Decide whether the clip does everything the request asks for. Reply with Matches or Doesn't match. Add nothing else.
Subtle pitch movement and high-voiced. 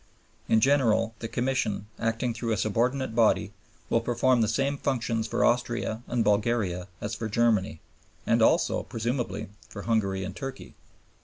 Doesn't match